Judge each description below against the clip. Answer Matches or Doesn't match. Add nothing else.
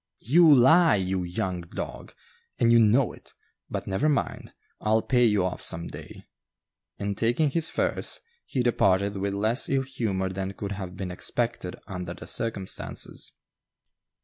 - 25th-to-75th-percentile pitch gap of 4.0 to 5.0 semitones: Matches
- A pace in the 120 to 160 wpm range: Matches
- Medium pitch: Doesn't match